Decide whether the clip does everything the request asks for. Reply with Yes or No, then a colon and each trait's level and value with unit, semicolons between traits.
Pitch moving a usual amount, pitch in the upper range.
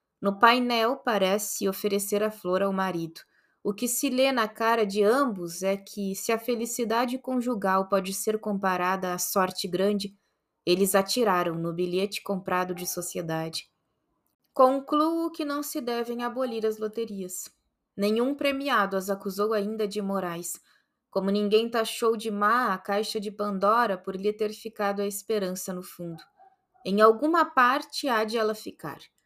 Yes: average, 3.5 semitones; high, 210 Hz